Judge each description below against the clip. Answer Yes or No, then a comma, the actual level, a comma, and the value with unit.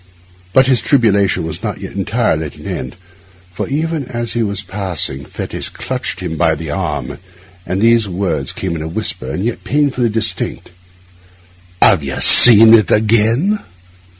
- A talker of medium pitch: No, low, 105 Hz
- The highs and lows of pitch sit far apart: Yes, wide, 6.0 semitones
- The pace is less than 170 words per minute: Yes, average, 160 wpm